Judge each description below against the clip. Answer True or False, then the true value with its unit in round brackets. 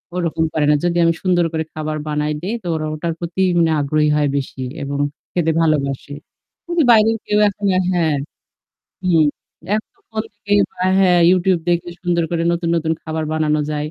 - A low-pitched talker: False (165 Hz)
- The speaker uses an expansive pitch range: False (2.8 semitones)